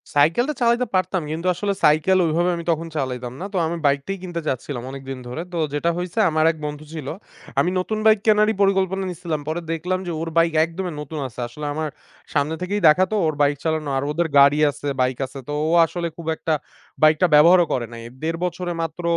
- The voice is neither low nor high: Yes, medium, 165 Hz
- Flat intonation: No, average, 3.5 semitones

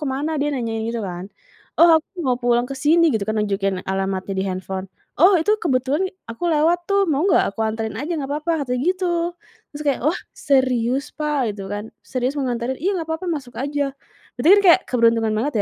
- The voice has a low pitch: No, very high, 260 Hz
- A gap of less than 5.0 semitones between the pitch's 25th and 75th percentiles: No, average, 5.3 semitones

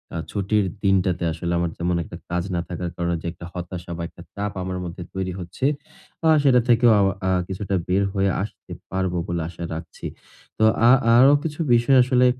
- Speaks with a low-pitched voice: Yes, very low, 95 Hz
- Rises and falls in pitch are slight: No, average, 3.3 semitones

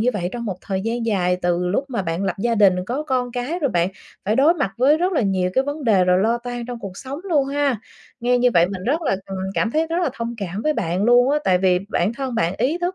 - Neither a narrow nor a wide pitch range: No, wide, 6.1 semitones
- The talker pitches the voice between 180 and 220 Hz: No, high, 235 Hz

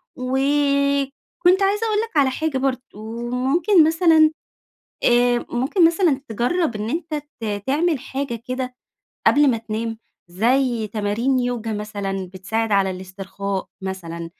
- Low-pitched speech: No, very high, 255 Hz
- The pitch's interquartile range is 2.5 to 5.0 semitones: No, wide, 5.5 semitones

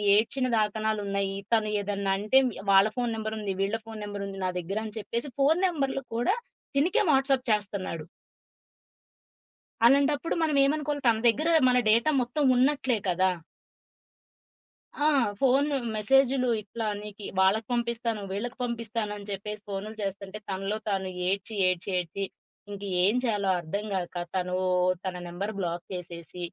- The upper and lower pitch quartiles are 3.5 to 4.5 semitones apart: Yes, average, 4.2 semitones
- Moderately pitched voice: No, high, 215 Hz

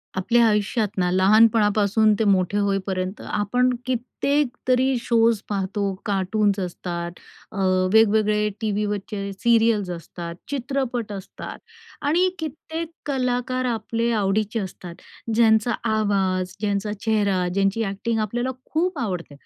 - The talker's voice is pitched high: Yes, high, 210 Hz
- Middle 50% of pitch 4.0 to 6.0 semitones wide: No, average, 3.2 semitones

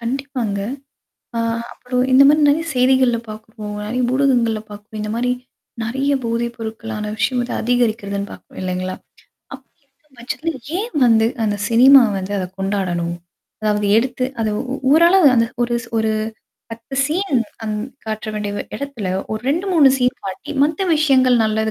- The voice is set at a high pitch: Yes, high, 235 Hz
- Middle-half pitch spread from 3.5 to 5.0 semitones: Yes, average, 3.9 semitones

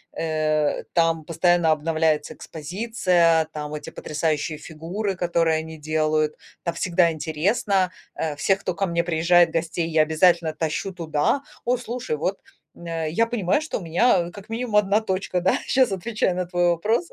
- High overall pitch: No, medium, 170 Hz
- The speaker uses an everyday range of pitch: Yes, average, 3.3 semitones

